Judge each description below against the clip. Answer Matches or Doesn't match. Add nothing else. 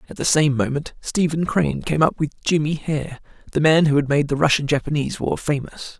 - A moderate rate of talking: Doesn't match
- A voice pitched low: Doesn't match